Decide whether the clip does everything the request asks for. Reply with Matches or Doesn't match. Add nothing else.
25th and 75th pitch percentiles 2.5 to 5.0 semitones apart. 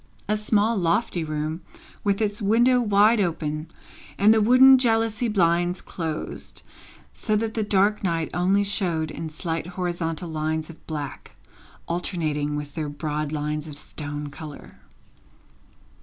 Doesn't match